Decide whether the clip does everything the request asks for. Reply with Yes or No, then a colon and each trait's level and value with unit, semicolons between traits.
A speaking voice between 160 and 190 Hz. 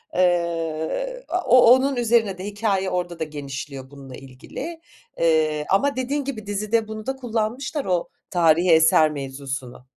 Yes: medium, 185 Hz